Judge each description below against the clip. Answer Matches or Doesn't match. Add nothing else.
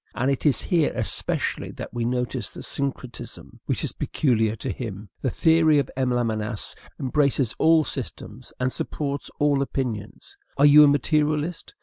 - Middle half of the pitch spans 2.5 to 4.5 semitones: Matches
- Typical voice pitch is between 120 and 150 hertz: Matches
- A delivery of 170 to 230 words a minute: Doesn't match